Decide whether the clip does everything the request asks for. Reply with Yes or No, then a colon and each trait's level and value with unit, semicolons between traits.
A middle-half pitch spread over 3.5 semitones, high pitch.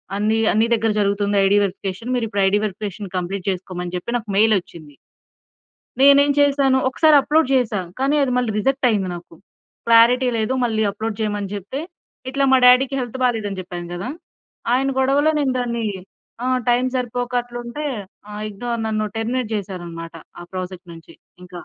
Yes: average, 4.5 semitones; high, 225 Hz